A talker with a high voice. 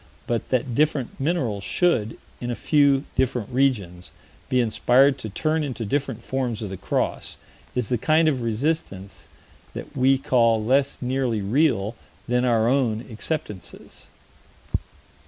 No: low, 125 Hz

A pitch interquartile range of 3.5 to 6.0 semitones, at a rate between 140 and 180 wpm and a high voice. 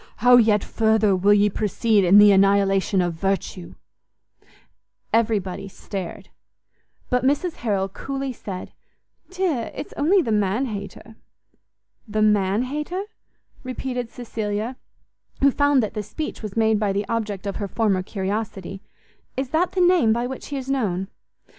Yes: average, 4.4 semitones; average, 145 wpm; high, 215 Hz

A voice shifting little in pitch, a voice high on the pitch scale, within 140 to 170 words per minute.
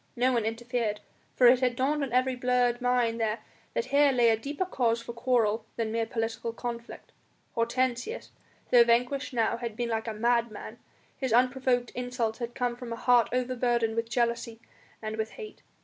No: narrow, 1.6 semitones; high, 240 Hz; average, 180 wpm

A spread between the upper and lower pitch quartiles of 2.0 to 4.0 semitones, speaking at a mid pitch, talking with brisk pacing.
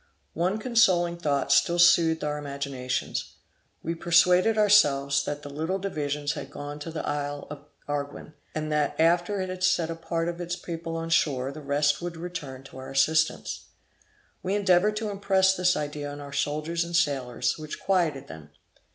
No: average, 3.5 semitones; medium, 160 Hz; average, 175 wpm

